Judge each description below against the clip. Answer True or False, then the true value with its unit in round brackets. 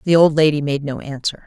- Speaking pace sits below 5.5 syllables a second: False (5.9 syllables/s)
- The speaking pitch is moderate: True (150 Hz)